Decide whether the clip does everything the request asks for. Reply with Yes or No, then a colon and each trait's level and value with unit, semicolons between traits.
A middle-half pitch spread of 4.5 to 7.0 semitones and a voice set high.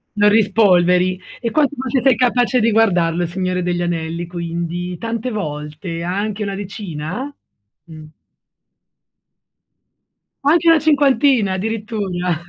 Yes: average, 5.0 semitones; high, 195 Hz